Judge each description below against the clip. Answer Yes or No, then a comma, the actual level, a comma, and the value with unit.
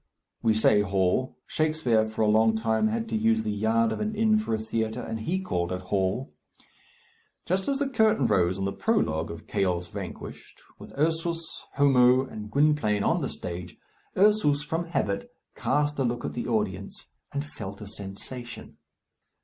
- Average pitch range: No, wide, 6.4 semitones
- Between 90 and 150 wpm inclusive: No, average, 175 wpm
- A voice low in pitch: Yes, low, 115 Hz